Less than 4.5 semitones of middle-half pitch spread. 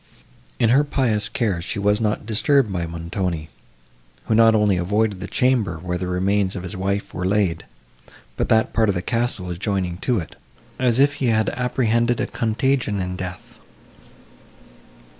Yes: average, 4.1 semitones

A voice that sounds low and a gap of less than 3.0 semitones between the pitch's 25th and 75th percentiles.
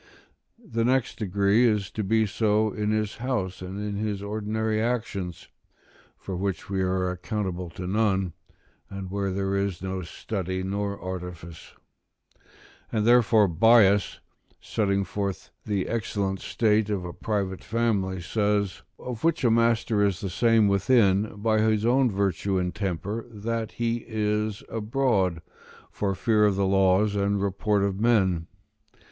Yes: low, 100 Hz; narrow, 2.5 semitones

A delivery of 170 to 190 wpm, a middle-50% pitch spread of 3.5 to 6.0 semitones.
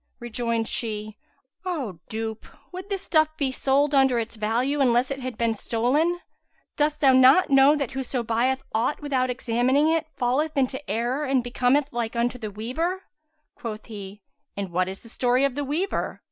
Yes: average, 175 wpm; average, 3.9 semitones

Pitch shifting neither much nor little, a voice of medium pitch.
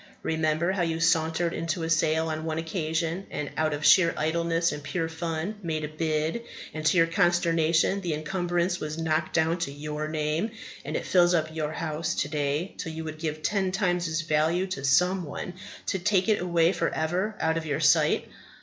No: narrow, 1.9 semitones; medium, 160 Hz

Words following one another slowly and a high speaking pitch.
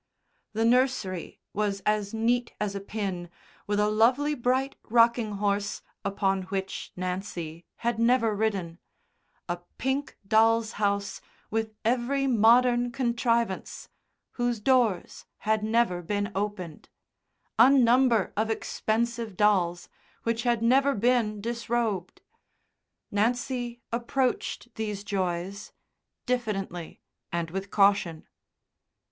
Yes: slow, 105 wpm; high, 220 Hz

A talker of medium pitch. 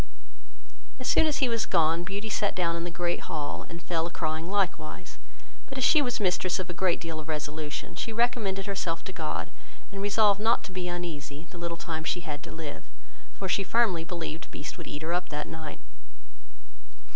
Yes: medium, 175 Hz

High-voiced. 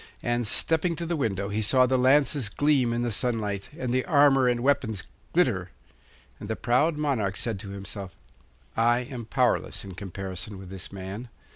No: low, 120 Hz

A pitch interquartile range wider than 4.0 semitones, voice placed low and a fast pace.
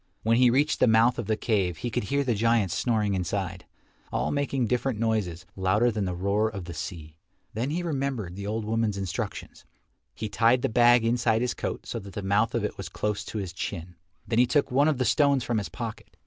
No: average, 3.7 semitones; low, 110 Hz; fast, 225 wpm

